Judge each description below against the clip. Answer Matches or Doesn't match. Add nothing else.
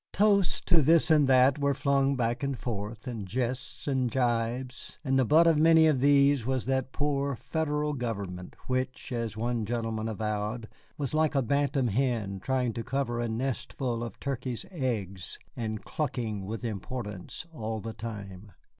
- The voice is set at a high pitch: Doesn't match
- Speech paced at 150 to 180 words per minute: Matches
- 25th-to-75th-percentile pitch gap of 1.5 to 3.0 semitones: Doesn't match